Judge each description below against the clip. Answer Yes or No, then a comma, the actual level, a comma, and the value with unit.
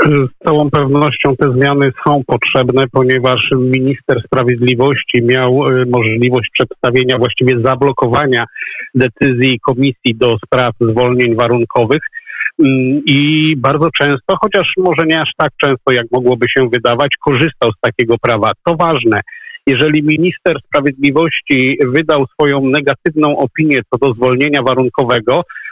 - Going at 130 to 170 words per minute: No, average, 120 wpm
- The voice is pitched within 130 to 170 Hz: Yes, low, 135 Hz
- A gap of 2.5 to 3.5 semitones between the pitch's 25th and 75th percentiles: Yes, average, 2.8 semitones